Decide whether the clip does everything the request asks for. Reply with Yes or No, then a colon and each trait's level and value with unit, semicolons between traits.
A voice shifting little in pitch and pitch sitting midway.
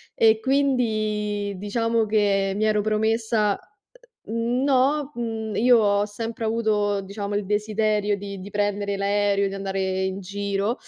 No: narrow, 1.8 semitones; high, 210 Hz